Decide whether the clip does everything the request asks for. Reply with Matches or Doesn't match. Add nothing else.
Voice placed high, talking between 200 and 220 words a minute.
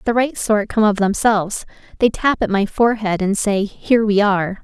Matches